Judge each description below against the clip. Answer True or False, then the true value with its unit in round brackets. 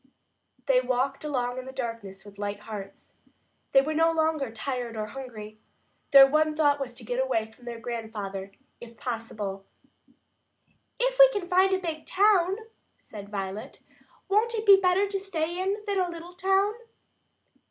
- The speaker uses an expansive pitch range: True (8.2 semitones)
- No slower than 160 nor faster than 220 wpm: True (165 wpm)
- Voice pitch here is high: True (270 Hz)